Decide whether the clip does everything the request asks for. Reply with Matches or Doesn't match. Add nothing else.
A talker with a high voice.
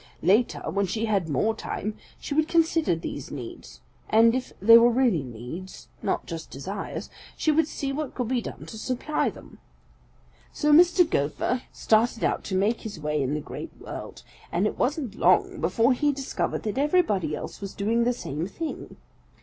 Matches